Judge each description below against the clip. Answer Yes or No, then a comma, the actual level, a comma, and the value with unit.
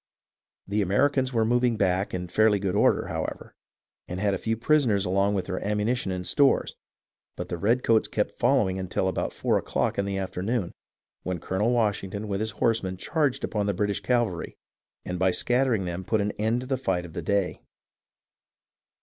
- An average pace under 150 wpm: No, average, 190 wpm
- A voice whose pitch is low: Yes, low, 105 Hz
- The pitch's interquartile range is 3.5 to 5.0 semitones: Yes, average, 3.8 semitones